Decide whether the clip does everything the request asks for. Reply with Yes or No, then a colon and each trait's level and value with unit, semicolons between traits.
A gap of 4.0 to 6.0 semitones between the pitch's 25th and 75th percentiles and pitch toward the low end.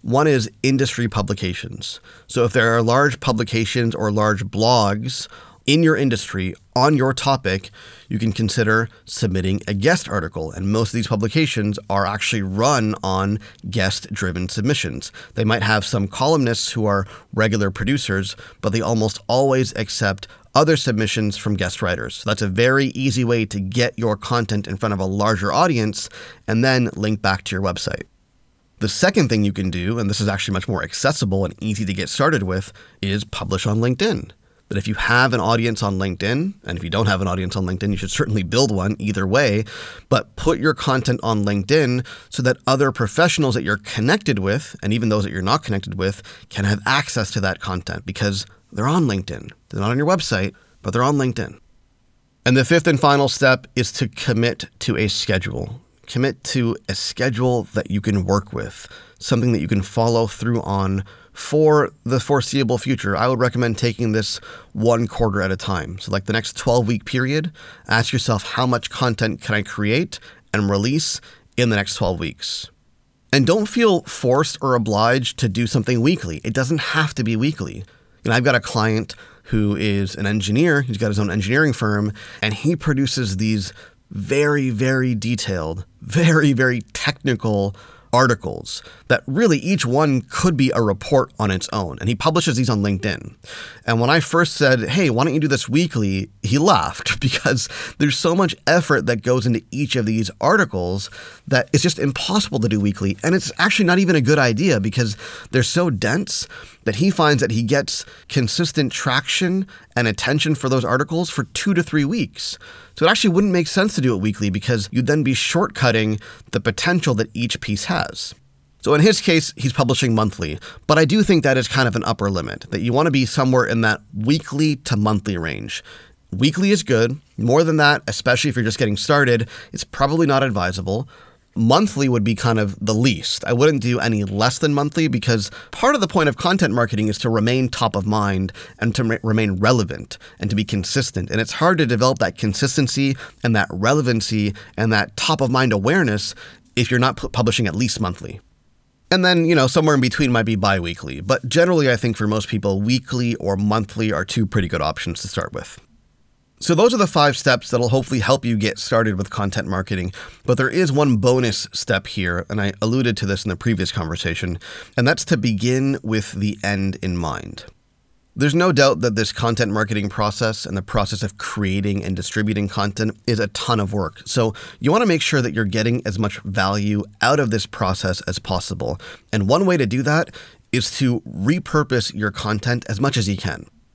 Yes: average, 4.7 semitones; low, 115 Hz